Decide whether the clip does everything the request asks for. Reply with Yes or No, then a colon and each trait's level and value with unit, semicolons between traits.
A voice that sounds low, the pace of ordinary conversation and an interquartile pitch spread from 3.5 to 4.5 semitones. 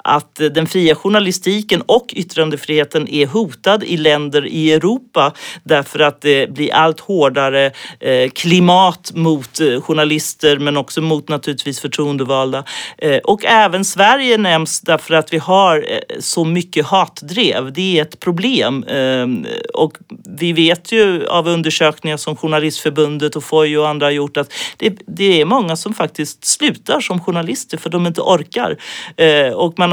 No: medium, 160 Hz; average, 140 wpm; average, 4.0 semitones